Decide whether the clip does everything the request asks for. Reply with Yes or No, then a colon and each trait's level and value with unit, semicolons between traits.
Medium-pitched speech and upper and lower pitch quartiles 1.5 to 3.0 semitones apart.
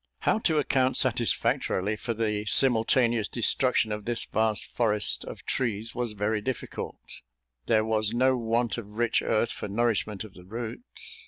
No: low, 115 Hz; narrow, 2.4 semitones